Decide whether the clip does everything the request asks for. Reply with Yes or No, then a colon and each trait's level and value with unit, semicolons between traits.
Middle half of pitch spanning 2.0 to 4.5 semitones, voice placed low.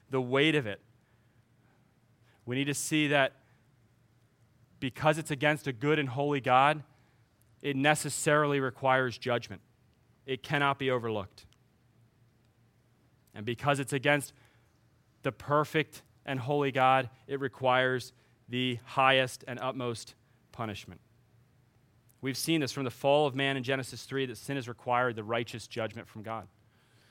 Yes: average, 2.8 semitones; low, 125 Hz